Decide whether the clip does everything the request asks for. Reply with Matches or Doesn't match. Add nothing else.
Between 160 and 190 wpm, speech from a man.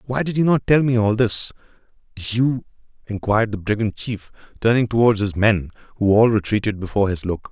Matches